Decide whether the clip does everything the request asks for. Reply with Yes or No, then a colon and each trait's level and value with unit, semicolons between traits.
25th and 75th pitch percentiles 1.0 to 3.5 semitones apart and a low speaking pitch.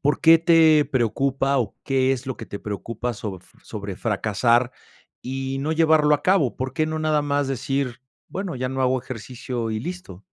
No: average, 4.2 semitones; low, 130 Hz